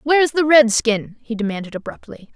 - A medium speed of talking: Yes, average, 180 wpm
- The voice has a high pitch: Yes, high, 245 Hz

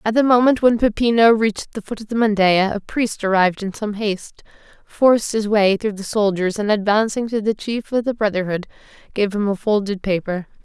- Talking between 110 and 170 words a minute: No, fast, 205 wpm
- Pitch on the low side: No, high, 210 Hz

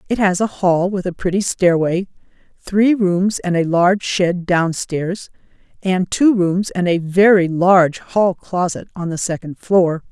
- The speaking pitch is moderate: Yes, medium, 180 Hz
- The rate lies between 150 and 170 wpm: Yes, average, 165 wpm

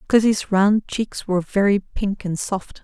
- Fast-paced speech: No, average, 170 wpm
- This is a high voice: Yes, high, 200 Hz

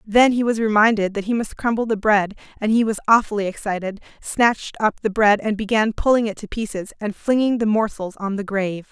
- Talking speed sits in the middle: No, fast, 215 wpm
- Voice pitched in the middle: No, high, 215 Hz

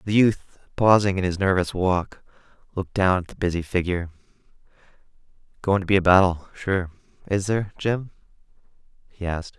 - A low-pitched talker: Yes, very low, 95 Hz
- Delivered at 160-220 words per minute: No, average, 150 wpm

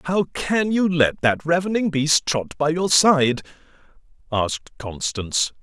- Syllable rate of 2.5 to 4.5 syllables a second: Yes, 4.1 syllables/s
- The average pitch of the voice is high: No, medium, 155 Hz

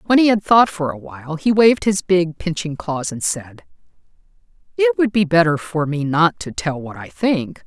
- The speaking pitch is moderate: Yes, medium, 175 Hz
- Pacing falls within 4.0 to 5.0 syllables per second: Yes, 4.8 syllables/s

